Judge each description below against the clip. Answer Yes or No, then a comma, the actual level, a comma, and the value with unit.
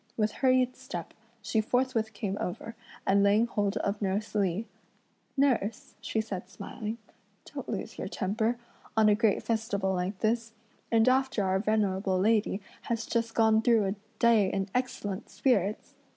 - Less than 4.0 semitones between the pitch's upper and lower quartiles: Yes, narrow, 2.5 semitones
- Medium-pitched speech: No, high, 215 Hz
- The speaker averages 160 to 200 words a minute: No, average, 150 wpm